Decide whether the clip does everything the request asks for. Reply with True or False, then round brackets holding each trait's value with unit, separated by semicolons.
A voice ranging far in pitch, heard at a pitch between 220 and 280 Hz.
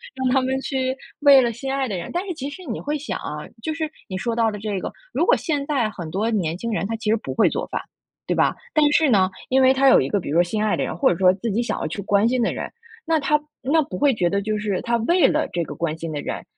True (5.7 semitones; 235 Hz)